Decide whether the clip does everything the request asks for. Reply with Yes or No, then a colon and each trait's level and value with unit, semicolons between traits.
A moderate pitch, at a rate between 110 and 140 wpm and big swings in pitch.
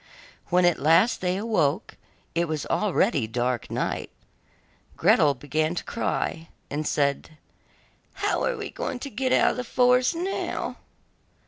Yes: medium, 175 Hz; slow, 135 wpm; wide, 8.6 semitones